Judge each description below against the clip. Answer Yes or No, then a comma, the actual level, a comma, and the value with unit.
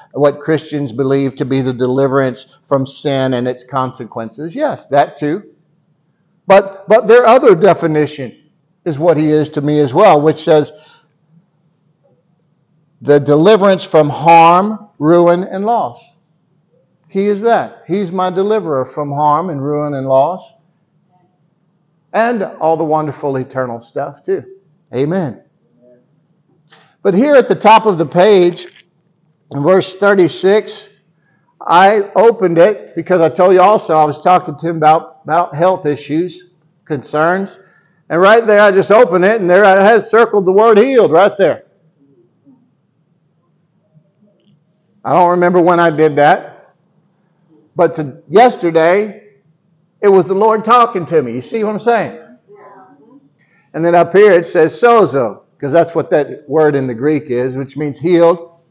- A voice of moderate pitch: Yes, medium, 170 Hz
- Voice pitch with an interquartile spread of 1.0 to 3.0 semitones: No, average, 3.8 semitones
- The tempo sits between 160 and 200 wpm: No, average, 145 wpm